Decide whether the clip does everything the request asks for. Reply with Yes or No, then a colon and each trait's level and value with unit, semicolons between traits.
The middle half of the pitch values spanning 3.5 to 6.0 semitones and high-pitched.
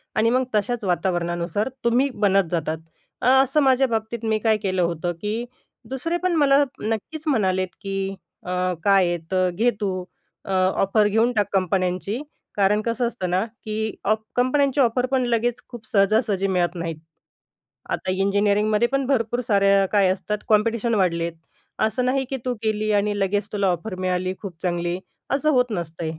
Yes: average, 4.2 semitones; high, 210 Hz